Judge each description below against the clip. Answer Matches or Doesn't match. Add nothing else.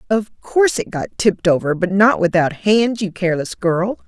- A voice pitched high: Matches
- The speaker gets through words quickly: Doesn't match